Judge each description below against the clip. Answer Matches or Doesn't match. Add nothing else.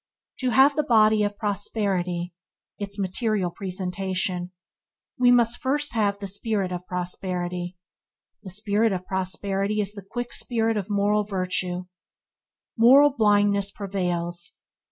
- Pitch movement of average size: Matches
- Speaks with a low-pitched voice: Doesn't match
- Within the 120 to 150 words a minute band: Matches